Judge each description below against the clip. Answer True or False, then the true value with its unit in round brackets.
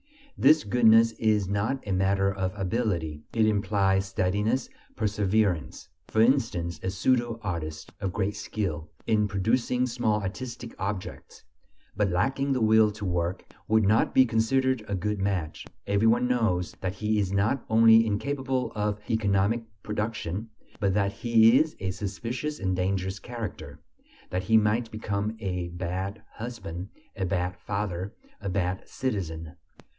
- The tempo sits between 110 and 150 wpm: True (145 wpm)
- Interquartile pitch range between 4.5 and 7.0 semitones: False (3.2 semitones)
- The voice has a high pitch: False (105 Hz)